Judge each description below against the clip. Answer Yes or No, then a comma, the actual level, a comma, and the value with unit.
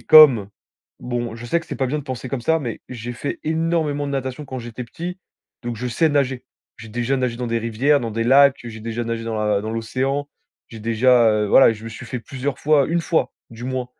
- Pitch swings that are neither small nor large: Yes, average, 3.5 semitones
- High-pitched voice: No, low, 125 Hz